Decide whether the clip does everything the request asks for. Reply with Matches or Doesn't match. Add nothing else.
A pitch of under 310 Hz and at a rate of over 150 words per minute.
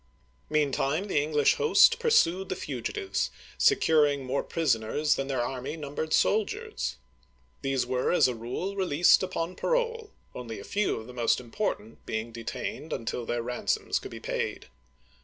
Matches